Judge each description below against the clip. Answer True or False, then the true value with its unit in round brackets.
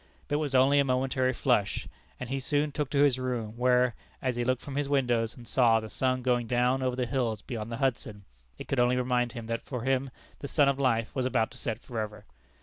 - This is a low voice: True (125 Hz)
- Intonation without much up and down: True (2.2 semitones)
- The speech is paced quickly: True (240 wpm)